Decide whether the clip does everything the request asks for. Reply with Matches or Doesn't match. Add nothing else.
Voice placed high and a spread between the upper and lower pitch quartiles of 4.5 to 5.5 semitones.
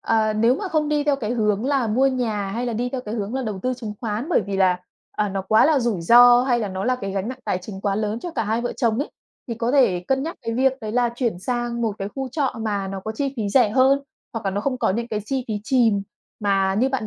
Doesn't match